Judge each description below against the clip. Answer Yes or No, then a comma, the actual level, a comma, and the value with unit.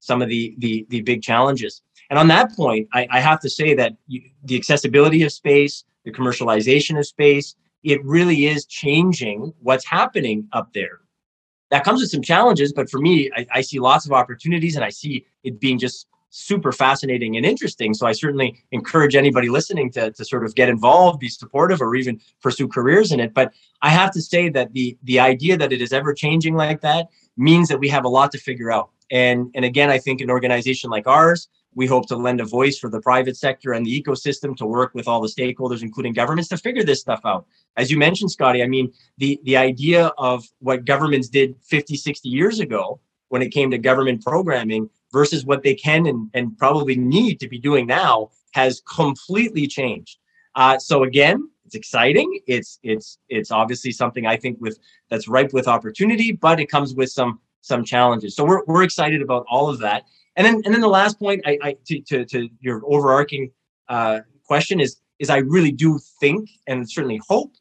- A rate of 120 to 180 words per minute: No, fast, 205 wpm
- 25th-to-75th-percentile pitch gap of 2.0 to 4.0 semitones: Yes, average, 3.3 semitones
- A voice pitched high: No, low, 135 Hz